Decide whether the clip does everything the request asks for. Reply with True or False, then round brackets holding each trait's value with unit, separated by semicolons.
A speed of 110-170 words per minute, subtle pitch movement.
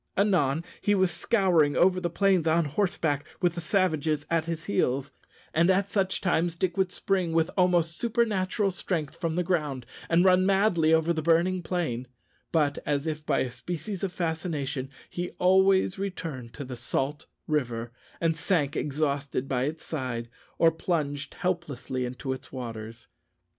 False (160 wpm; 4.3 semitones)